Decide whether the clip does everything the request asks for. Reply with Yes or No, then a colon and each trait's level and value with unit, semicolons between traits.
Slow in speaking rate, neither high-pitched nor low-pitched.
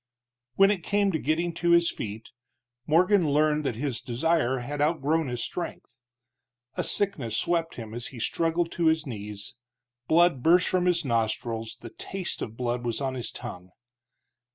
No: average, 165 wpm; medium, 145 Hz